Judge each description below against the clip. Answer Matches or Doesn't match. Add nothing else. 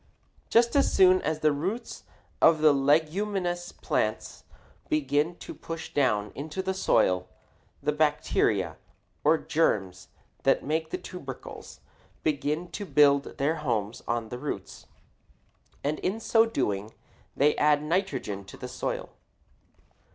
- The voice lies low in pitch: Doesn't match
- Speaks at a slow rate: Matches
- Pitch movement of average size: Matches